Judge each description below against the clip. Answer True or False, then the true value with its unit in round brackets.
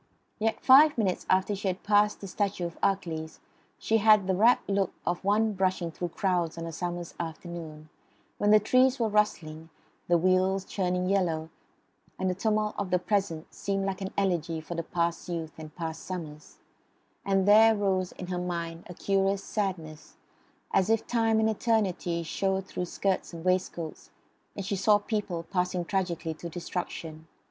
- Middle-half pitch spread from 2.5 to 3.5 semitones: True (3.1 semitones)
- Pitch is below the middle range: False (185 Hz)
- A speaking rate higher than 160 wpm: True (170 wpm)